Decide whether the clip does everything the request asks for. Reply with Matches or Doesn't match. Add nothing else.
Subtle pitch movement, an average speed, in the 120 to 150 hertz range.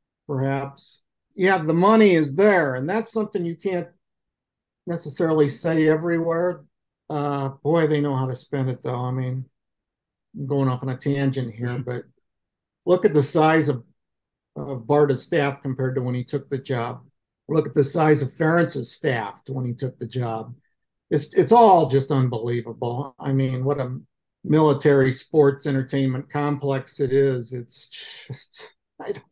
Doesn't match